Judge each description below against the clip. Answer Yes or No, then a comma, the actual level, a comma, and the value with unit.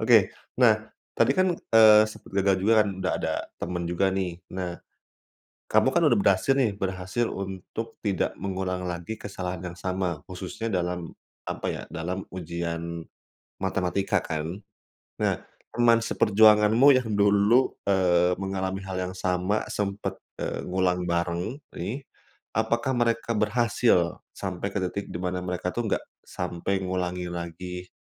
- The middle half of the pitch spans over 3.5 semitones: No, average, 3.0 semitones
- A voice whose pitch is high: No, very low, 95 Hz